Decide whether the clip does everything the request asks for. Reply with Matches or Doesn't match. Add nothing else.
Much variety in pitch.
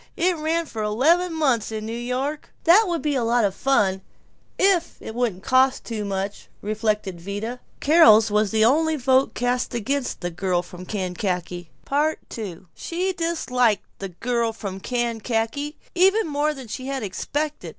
Matches